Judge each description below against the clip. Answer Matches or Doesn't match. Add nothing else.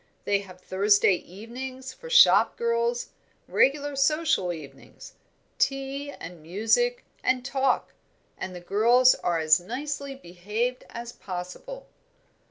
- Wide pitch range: Matches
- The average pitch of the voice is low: Doesn't match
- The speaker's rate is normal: Doesn't match